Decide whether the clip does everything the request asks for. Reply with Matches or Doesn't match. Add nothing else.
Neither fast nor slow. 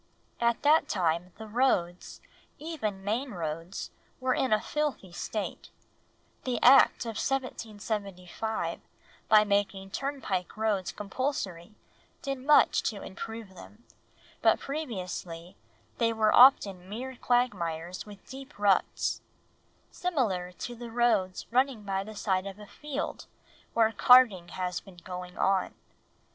Doesn't match